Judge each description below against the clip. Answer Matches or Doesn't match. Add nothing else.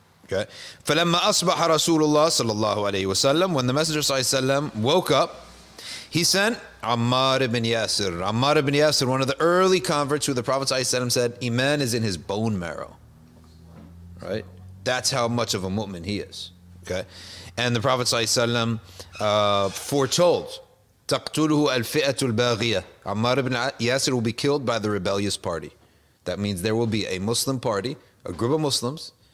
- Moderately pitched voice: Doesn't match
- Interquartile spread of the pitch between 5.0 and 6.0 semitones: Matches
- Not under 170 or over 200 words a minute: Doesn't match